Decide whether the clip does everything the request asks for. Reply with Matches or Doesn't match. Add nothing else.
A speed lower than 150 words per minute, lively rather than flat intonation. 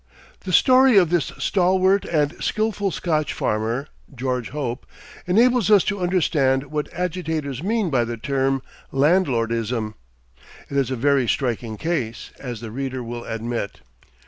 Matches